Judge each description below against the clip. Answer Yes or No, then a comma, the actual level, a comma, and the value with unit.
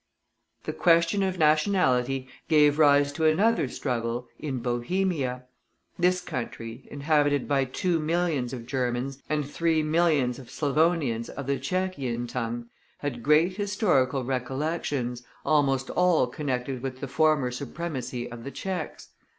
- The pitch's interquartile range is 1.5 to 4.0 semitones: No, average, 4.4 semitones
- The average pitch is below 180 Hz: Yes, medium, 140 Hz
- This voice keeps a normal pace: No, slow, 130 wpm